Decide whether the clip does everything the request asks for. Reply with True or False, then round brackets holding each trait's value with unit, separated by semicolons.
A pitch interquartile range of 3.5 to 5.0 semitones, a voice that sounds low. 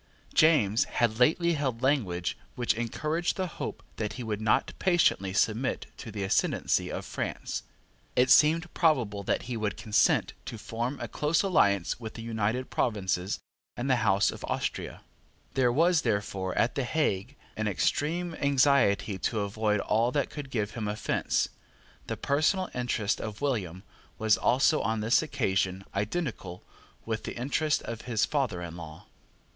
False (5.6 semitones; 115 Hz)